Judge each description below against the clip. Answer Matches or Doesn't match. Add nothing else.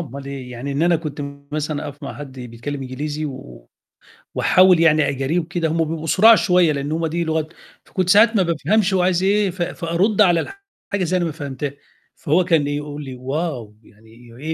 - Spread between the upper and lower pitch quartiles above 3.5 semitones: Matches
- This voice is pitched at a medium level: Matches